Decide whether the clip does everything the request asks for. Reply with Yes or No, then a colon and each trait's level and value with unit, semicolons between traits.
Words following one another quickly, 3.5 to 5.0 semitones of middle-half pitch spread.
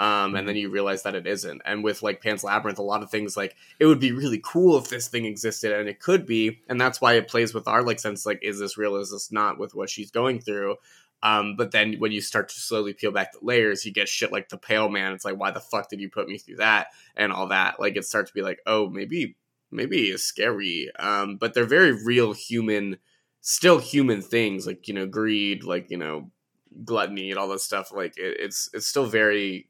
No: fast, 250 wpm; narrow, 2.5 semitones